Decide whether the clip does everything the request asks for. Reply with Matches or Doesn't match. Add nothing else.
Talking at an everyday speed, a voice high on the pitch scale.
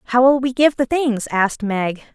Doesn't match